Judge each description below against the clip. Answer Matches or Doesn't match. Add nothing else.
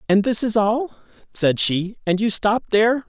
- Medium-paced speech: Matches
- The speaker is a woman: Doesn't match